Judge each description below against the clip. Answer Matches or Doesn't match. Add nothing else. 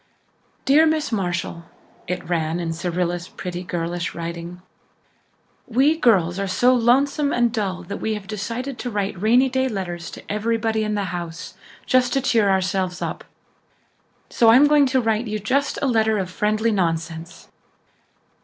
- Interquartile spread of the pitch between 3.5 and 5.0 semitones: Doesn't match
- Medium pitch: Doesn't match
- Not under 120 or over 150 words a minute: Doesn't match